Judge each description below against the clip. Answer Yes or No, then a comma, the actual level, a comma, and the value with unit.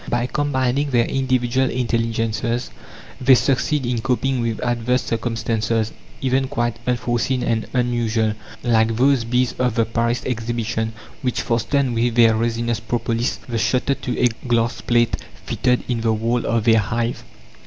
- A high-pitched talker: No, low, 120 Hz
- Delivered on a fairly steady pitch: Yes, narrow, 1.6 semitones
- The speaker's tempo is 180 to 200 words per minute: No, average, 145 wpm